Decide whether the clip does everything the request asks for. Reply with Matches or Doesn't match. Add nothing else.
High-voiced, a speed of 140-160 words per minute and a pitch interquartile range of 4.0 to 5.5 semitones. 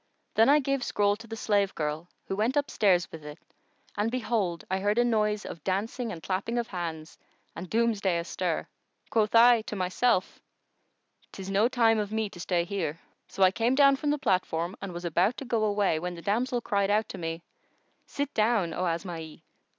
Doesn't match